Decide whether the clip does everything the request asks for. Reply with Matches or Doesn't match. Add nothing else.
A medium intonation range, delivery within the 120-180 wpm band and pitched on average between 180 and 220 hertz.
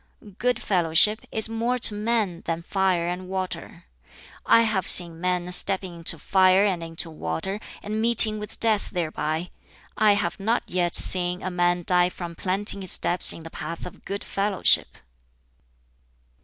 Matches